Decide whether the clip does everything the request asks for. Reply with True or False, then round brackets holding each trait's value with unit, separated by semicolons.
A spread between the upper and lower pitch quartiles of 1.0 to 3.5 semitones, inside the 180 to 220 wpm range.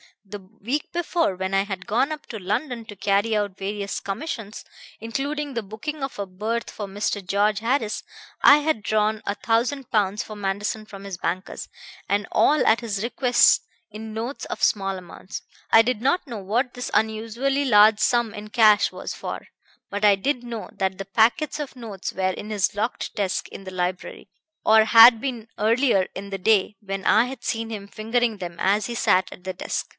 True (3.2 semitones; 190 wpm)